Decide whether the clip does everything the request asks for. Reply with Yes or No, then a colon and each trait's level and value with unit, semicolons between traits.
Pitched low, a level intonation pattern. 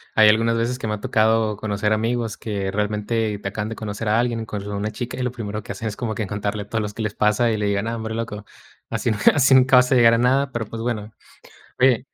Yes: low, 110 Hz; narrow, 1.9 semitones